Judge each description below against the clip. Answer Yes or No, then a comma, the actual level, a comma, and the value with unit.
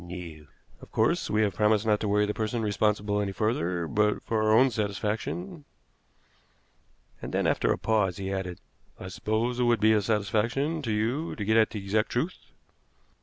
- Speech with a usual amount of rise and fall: No, narrow, 2.0 semitones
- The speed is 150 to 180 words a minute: No, average, 190 wpm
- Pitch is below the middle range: Yes, low, 105 Hz